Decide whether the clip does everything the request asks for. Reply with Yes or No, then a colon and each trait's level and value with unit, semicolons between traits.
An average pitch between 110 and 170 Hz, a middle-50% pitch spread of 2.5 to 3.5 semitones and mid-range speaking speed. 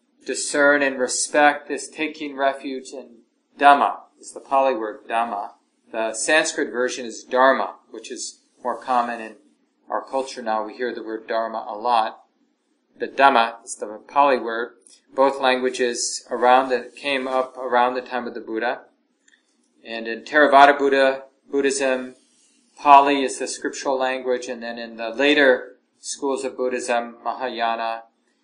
Yes: low, 130 Hz; average, 3.0 semitones; average, 150 wpm